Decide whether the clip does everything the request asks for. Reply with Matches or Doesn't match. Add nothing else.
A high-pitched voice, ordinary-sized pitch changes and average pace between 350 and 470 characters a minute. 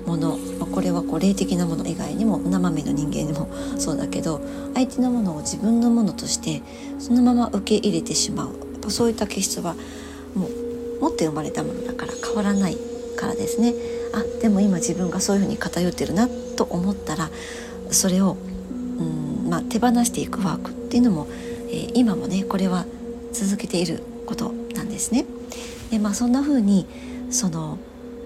Matches